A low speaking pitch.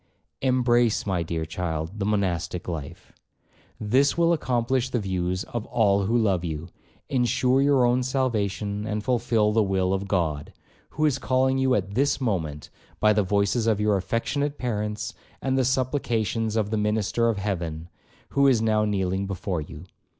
Yes: low, 105 Hz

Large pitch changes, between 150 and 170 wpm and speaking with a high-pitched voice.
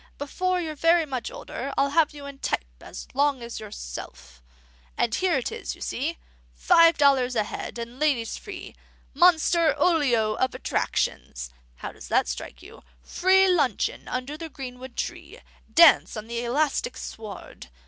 Yes: wide, 5.7 semitones; average, 160 wpm; very high, 275 Hz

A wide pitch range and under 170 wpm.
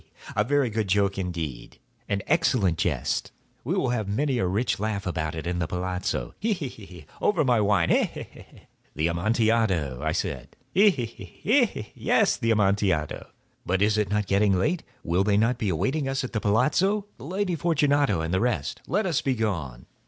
No: wide, 6.6 semitones; average, 180 wpm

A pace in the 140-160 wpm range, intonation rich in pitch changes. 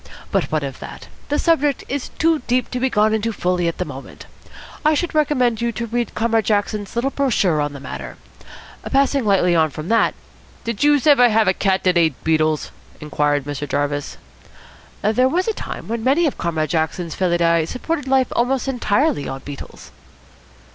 No: average, 185 wpm; wide, 8.7 semitones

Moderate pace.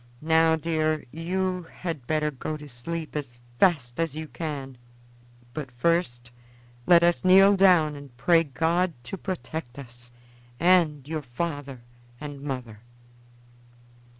No: slow, 125 wpm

